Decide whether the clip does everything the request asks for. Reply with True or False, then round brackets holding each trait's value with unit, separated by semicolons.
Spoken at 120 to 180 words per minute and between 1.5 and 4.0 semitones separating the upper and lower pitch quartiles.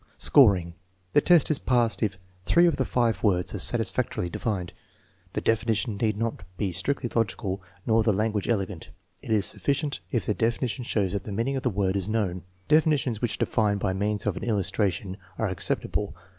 False (195 wpm; 3.5 semitones)